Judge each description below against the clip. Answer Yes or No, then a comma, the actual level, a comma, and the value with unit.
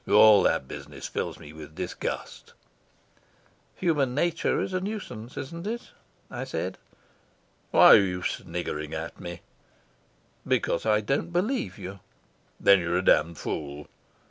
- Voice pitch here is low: Yes, low, 105 Hz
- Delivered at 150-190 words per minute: No, slow, 135 wpm